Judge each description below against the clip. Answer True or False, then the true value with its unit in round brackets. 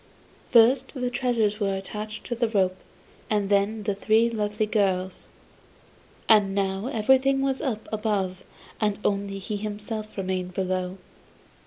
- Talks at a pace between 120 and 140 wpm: True (135 wpm)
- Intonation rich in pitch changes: False (2.5 semitones)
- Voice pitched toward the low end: False (210 Hz)